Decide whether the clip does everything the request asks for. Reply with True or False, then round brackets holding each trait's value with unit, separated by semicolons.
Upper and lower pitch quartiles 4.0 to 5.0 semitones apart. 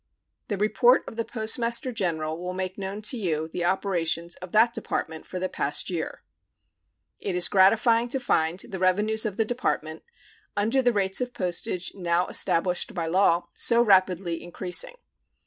True (4.3 semitones)